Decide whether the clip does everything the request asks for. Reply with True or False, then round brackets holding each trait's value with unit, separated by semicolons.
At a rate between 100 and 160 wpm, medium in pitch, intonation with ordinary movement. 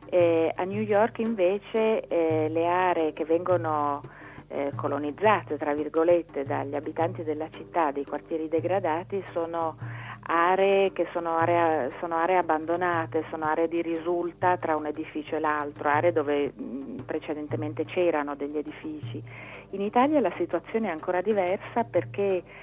True (140 wpm; 165 Hz; 3.0 semitones)